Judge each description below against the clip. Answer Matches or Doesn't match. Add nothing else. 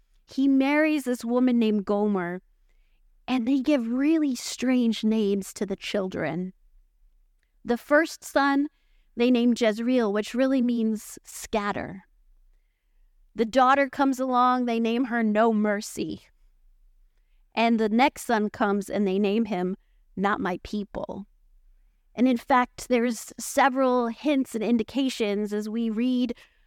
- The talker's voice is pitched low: Doesn't match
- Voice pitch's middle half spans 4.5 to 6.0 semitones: Doesn't match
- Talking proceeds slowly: Matches